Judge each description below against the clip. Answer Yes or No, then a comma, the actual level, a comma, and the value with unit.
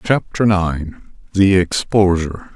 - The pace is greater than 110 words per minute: No, slow, 70 wpm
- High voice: No, very low, 95 Hz